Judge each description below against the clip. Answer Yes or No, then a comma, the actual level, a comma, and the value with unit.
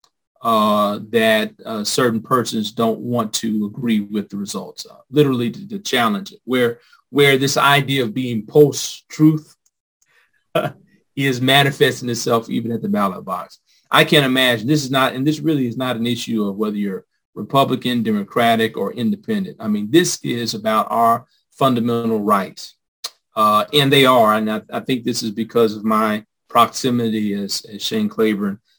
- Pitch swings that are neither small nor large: Yes, average, 4.7 semitones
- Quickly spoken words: No, average, 165 wpm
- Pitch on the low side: Yes, low, 120 Hz